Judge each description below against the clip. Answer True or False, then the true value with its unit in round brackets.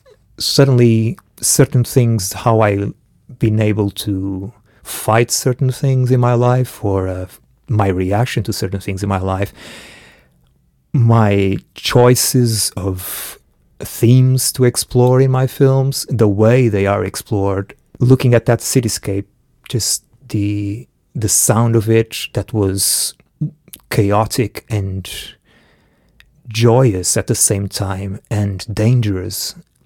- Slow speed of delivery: True (115 wpm)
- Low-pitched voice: True (110 Hz)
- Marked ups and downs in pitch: False (3.9 semitones)